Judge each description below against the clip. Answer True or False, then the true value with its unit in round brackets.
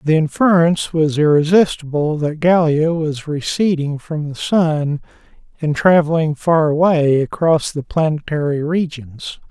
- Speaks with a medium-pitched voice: True (155 Hz)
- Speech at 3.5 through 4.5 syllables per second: True (4.3 syllables/s)